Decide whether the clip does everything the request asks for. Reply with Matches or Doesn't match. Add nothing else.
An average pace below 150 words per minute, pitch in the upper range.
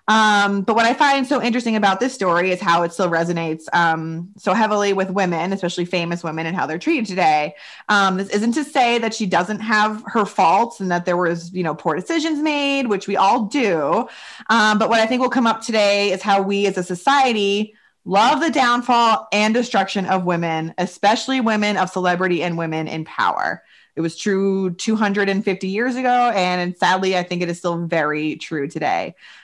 Doesn't match